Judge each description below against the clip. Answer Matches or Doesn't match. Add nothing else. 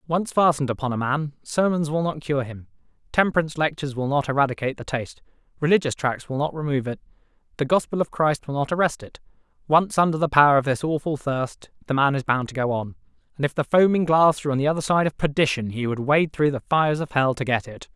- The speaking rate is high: Matches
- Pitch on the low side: Doesn't match